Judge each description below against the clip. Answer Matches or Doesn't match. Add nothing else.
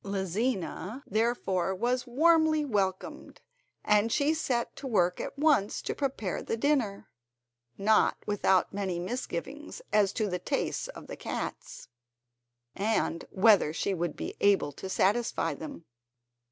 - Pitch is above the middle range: Matches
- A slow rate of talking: Matches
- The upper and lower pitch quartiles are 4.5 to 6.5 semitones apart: Matches